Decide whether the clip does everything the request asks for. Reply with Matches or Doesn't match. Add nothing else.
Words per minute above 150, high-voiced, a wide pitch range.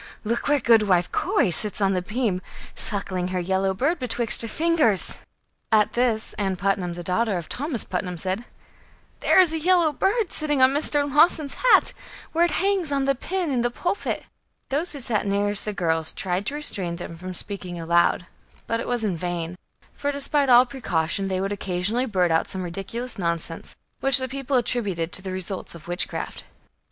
Matches